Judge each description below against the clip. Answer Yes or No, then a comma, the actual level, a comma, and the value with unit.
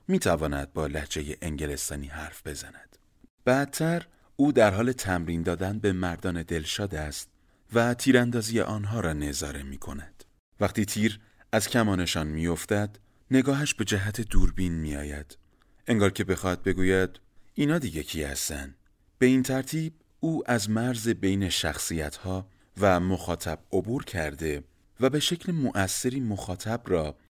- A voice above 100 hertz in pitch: No, very low, 95 Hz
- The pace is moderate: Yes, average, 140 wpm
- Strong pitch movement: Yes, wide, 6.3 semitones